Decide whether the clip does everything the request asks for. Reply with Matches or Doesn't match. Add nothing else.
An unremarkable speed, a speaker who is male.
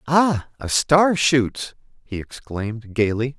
Doesn't match